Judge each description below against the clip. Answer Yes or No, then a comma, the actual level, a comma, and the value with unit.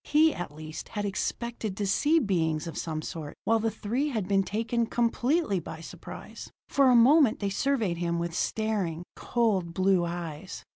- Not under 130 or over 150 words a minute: No, average, 175 wpm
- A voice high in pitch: Yes, high, 200 Hz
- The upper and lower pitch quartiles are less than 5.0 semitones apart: No, wide, 5.6 semitones